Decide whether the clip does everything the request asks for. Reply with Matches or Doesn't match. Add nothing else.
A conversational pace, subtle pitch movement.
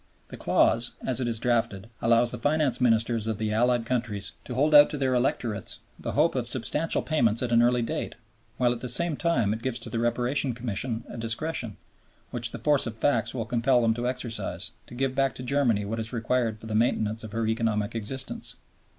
Doesn't match